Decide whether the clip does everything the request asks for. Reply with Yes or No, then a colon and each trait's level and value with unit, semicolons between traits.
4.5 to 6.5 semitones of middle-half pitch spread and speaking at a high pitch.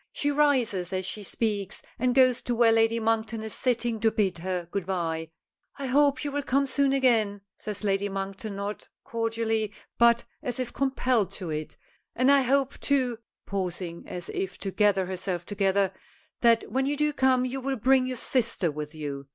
Yes: average, 4.9 semitones; high, 225 Hz